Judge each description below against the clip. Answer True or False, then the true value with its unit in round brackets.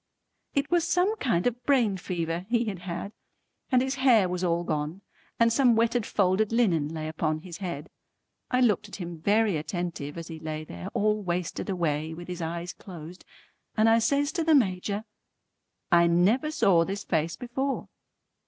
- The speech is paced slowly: False (175 wpm)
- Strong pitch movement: True (5.7 semitones)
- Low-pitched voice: False (185 Hz)